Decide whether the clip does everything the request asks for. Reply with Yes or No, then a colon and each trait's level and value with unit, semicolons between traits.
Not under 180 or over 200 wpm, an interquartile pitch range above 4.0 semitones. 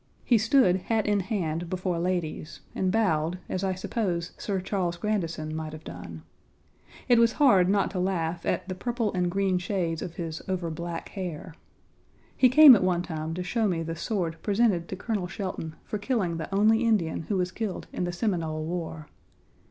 No: average, 185 wpm; average, 3.7 semitones